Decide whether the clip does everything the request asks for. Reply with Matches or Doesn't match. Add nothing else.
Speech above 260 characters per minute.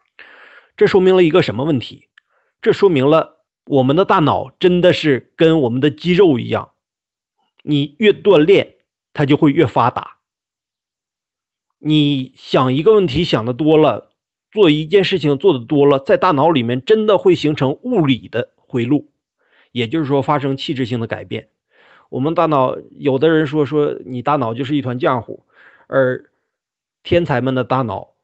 Doesn't match